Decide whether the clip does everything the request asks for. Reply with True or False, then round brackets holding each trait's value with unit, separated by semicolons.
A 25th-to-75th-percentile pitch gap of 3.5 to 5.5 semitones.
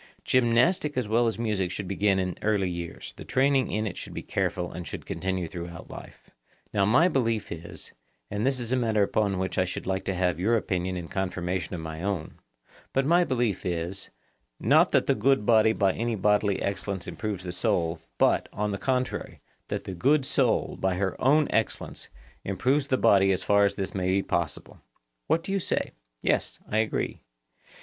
True (4.3 semitones)